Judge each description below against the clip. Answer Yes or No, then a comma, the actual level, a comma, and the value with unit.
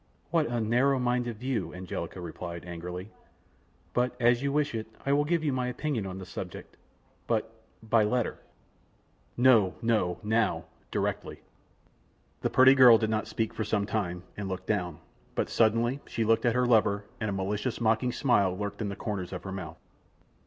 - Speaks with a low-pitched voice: Yes, low, 110 Hz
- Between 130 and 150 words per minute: No, average, 175 wpm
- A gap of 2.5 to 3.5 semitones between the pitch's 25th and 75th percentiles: No, average, 4.3 semitones